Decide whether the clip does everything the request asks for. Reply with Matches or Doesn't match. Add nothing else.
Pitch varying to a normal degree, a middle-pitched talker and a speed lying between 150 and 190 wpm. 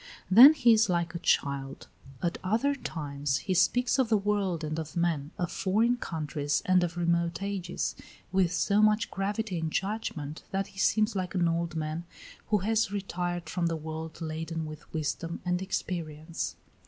Matches